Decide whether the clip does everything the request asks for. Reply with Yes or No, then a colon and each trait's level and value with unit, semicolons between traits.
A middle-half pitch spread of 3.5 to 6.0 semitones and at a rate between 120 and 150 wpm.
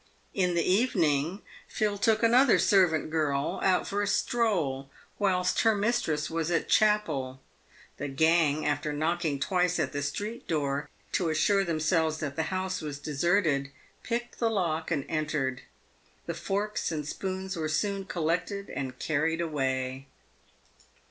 Yes: average, 4.8 semitones; average, 145 wpm